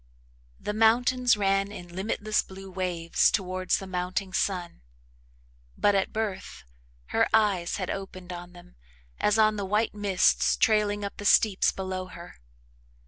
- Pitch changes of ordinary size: No, narrow, 2.3 semitones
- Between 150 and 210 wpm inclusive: No, average, 140 wpm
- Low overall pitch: No, high, 195 Hz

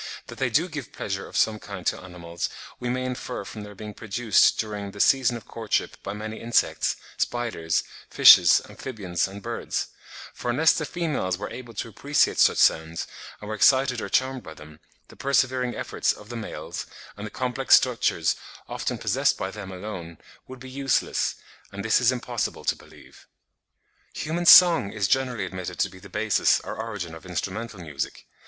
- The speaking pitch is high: No, low, 110 Hz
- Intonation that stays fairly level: No, average, 5.0 semitones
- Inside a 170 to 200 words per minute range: Yes, average, 180 wpm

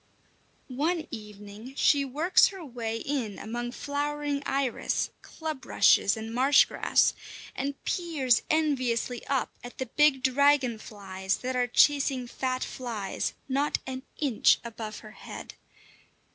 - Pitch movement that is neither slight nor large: Yes, average, 3.9 semitones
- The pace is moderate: No, slow, 130 wpm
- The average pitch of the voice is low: No, very high, 260 Hz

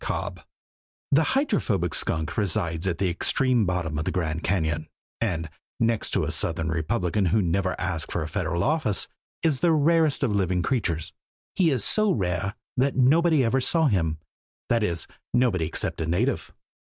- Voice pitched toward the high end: No, very low, 95 Hz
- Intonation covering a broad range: Yes, wide, 7.7 semitones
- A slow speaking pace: No, average, 165 wpm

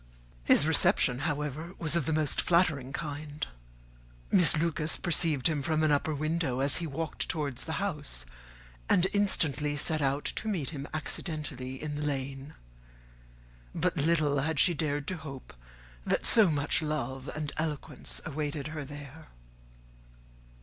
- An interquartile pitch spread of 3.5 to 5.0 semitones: No, narrow, 2.4 semitones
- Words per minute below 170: Yes, average, 145 wpm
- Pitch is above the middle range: No, medium, 150 Hz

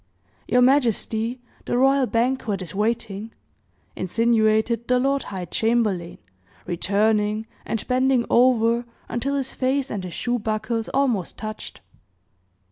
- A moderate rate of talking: No, slow, 120 wpm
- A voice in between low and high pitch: No, high, 230 Hz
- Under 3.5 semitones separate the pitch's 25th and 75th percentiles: Yes, average, 2.8 semitones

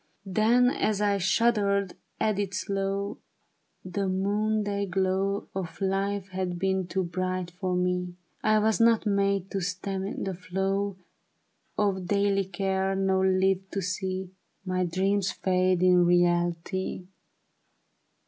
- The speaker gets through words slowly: Yes, slow, 130 wpm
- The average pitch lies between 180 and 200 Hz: Yes, high, 190 Hz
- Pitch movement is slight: Yes, narrow, 1.4 semitones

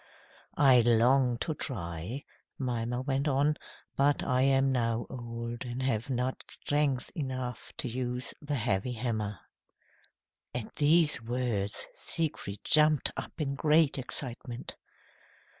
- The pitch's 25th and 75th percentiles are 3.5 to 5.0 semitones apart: No, average, 2.8 semitones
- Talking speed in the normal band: No, slow, 120 wpm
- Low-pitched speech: Yes, low, 125 Hz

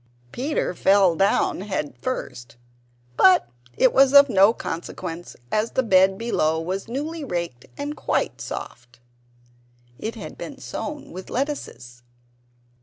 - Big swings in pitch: Yes, wide, 7.7 semitones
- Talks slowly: Yes, slow, 125 wpm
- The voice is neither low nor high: No, high, 195 Hz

